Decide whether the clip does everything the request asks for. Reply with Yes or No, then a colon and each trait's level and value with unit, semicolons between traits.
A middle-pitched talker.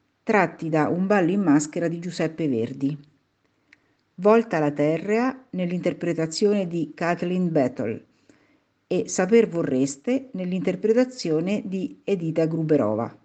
Yes: medium, 170 Hz